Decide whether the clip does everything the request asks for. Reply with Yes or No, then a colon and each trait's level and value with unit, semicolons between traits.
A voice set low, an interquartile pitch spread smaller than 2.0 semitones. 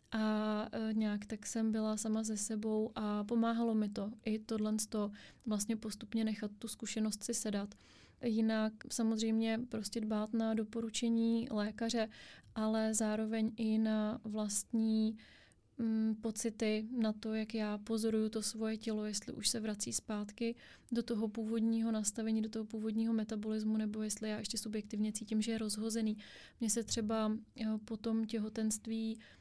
No: high, 220 Hz; narrow, 0.8 semitones